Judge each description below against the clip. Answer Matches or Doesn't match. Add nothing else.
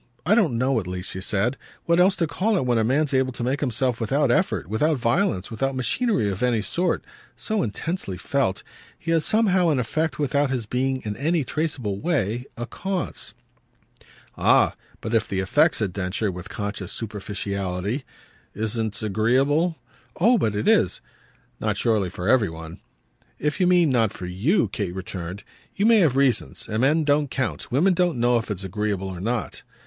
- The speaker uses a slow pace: Doesn't match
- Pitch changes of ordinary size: Doesn't match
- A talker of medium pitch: Doesn't match